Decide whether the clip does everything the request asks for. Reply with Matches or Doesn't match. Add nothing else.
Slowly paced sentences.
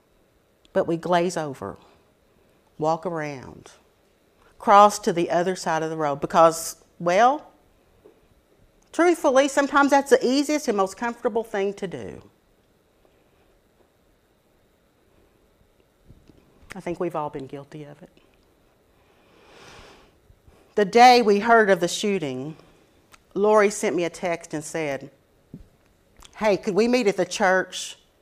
Matches